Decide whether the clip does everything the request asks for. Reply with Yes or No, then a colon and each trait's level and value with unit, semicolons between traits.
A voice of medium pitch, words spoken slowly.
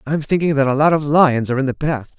No: medium, 145 Hz; fast, 305 wpm